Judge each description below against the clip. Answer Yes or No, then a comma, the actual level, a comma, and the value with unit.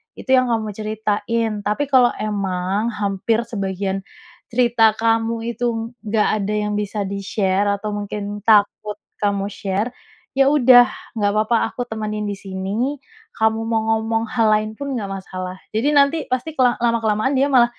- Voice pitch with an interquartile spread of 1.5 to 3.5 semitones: Yes, average, 2.7 semitones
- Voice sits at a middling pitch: No, high, 215 Hz